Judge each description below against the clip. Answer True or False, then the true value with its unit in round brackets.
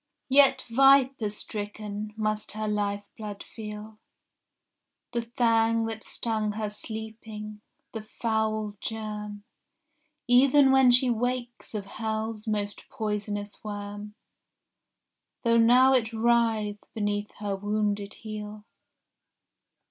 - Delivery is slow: True (100 wpm)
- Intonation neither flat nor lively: False (1.8 semitones)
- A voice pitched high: True (215 Hz)